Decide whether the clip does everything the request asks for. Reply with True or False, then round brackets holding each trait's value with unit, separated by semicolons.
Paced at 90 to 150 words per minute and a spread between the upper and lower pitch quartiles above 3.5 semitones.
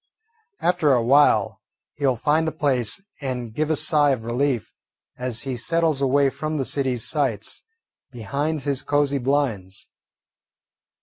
False (140 wpm; 3.2 semitones)